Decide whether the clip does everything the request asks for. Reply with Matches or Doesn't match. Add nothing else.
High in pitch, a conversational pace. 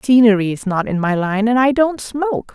Doesn't match